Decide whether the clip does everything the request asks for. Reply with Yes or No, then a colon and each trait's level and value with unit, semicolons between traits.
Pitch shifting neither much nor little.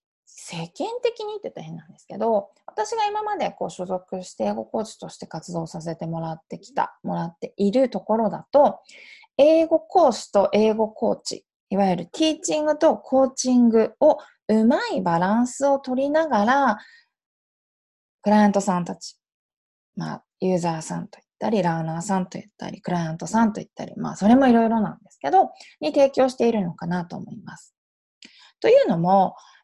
No: wide, 7.0 semitones